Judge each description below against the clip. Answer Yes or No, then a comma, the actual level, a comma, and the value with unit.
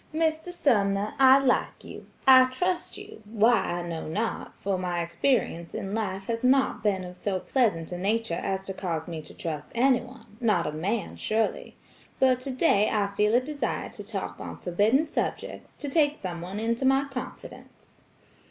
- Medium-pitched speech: No, high, 215 Hz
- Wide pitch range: Yes, wide, 5.7 semitones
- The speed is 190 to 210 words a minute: No, average, 170 wpm